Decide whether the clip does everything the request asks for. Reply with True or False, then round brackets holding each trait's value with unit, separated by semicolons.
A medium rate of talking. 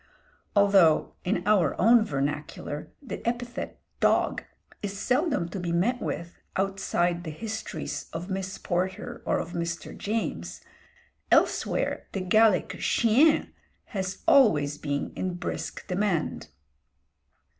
False (115 wpm)